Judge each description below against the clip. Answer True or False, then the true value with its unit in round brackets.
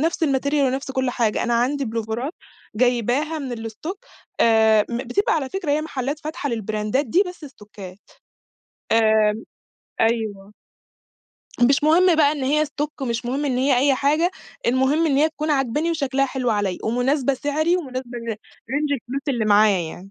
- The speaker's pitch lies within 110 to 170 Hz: False (265 Hz)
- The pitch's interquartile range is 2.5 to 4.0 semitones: False (4.5 semitones)